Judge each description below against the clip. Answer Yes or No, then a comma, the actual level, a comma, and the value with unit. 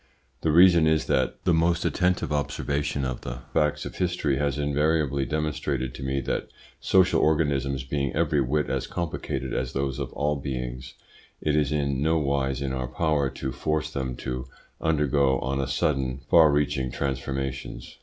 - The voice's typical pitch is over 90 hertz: No, very low, 70 Hz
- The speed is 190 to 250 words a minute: No, average, 165 wpm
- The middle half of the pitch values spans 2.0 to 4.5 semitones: Yes, narrow, 2.5 semitones